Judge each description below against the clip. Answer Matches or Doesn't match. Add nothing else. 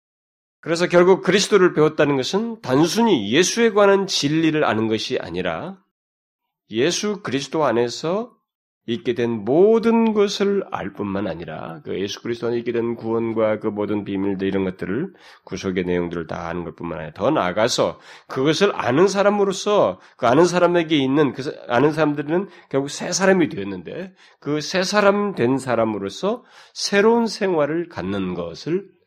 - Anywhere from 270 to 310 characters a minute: Doesn't match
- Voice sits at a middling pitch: Matches